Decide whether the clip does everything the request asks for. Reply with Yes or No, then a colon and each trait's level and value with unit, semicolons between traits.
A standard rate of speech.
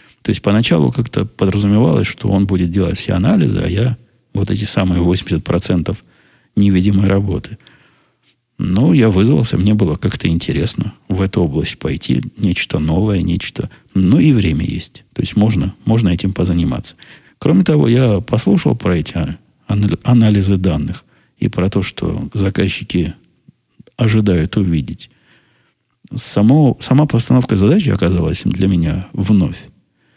Yes: average, 135 wpm